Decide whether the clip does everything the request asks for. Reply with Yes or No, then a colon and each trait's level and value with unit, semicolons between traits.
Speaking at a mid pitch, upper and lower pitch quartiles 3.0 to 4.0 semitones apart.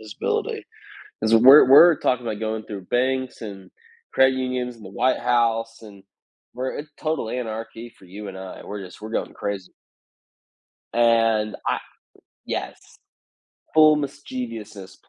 No: low, 115 Hz; average, 3.3 semitones